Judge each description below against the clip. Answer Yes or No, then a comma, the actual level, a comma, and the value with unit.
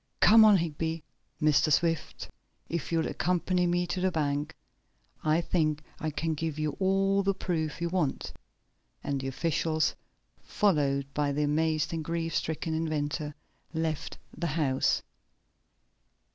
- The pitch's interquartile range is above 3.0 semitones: No, narrow, 2.4 semitones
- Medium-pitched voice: Yes, medium, 160 Hz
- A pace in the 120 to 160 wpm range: Yes, slow, 135 wpm